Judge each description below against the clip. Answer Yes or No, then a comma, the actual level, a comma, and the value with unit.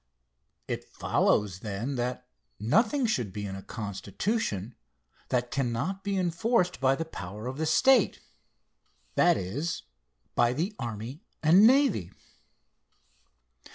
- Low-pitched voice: Yes, low, 130 Hz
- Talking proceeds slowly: Yes, slow, 120 wpm